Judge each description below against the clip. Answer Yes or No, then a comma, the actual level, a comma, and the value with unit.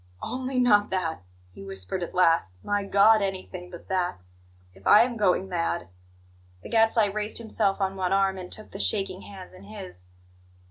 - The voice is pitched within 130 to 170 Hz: No, high, 190 Hz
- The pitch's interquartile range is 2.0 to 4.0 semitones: Yes, average, 2.9 semitones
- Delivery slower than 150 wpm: No, average, 180 wpm